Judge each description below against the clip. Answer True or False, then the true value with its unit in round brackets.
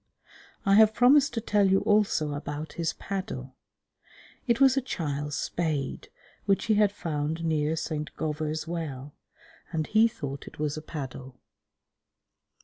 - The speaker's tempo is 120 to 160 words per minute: True (145 wpm)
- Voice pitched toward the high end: False (160 Hz)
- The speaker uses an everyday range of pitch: False (5.8 semitones)